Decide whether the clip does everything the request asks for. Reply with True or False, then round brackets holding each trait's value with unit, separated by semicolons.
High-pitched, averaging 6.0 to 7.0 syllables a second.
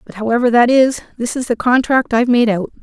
True (240 Hz; 6.1 syllables/s)